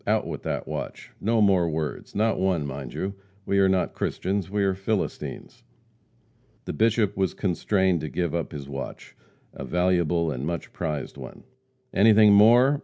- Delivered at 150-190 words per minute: Yes, average, 165 wpm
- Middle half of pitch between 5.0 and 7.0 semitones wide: No, average, 3.8 semitones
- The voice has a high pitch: No, very low, 95 Hz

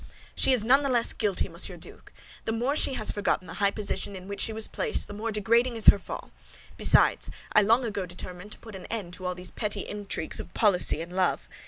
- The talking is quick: Yes, fast, 230 wpm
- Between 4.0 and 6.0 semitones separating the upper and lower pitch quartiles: No, average, 3.4 semitones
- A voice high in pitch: Yes, high, 210 Hz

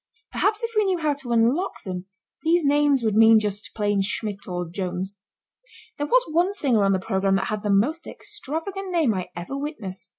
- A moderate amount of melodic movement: No, wide, 8.3 semitones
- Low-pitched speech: No, high, 225 Hz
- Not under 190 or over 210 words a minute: Yes, average, 195 wpm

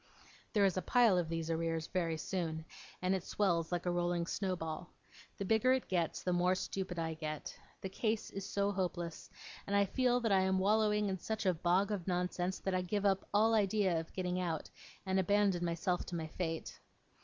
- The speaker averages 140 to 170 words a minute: No, average, 200 wpm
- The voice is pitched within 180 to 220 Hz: Yes, medium, 185 Hz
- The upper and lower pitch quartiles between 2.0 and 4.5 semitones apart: Yes, average, 2.8 semitones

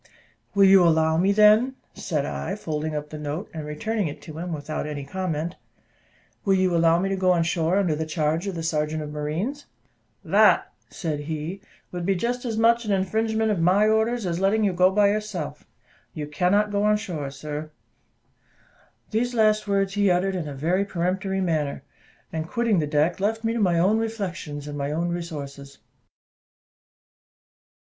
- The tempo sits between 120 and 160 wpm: No, average, 180 wpm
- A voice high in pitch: No, medium, 180 Hz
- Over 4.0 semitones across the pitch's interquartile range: Yes, average, 4.8 semitones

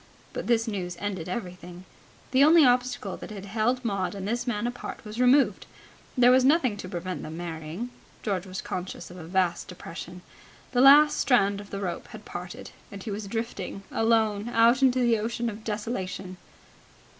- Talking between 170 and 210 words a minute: Yes, average, 180 wpm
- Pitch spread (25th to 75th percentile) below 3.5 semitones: No, average, 4.6 semitones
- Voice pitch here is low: No, high, 210 Hz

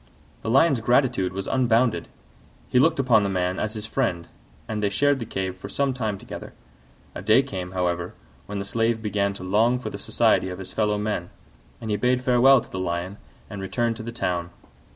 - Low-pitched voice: Yes, low, 105 Hz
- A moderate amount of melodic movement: Yes, average, 4.5 semitones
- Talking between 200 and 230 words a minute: Yes, fast, 205 wpm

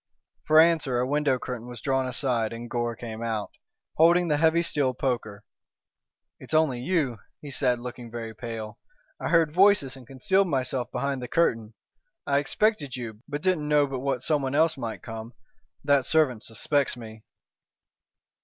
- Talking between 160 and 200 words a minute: Yes, average, 165 wpm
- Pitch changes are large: No, average, 4.1 semitones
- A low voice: Yes, low, 130 Hz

